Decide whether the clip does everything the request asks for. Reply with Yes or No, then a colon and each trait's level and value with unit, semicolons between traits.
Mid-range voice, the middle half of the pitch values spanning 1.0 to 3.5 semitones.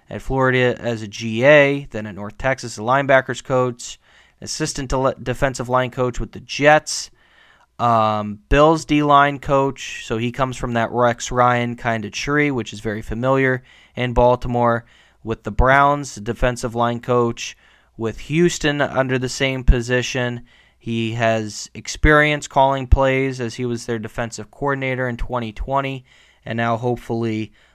No: low, 125 Hz; narrow, 2.6 semitones